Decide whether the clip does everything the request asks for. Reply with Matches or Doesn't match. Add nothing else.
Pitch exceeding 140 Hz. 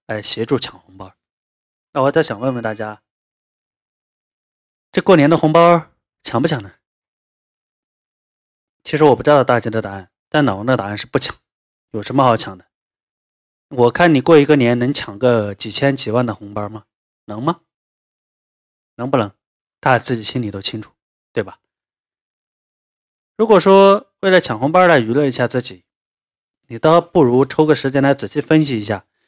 Doesn't match